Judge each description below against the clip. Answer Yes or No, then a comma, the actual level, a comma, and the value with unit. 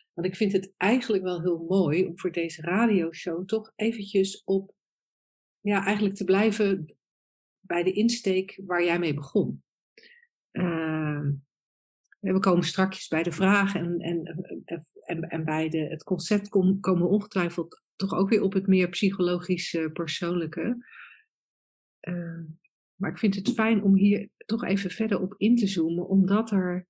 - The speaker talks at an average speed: Yes, average, 155 wpm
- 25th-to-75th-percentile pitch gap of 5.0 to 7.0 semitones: No, average, 3.0 semitones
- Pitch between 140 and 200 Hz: Yes, medium, 185 Hz